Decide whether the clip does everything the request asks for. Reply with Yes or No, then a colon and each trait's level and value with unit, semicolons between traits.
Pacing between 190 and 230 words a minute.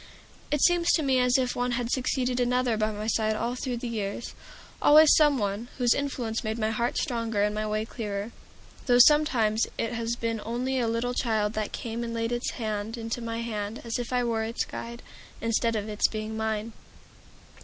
Yes: average, 200 wpm